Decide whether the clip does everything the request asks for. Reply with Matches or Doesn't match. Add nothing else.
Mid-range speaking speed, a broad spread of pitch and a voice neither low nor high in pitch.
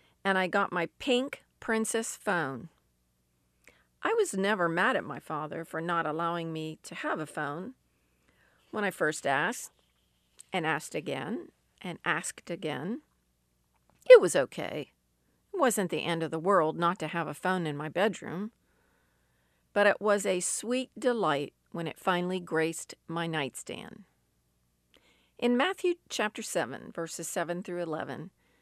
Matches